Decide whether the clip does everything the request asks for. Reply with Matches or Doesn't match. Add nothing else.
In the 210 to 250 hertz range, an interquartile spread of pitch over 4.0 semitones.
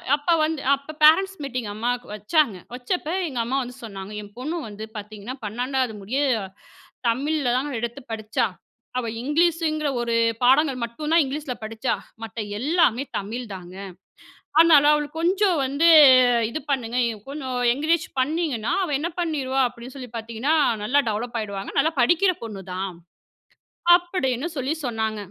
Doesn't match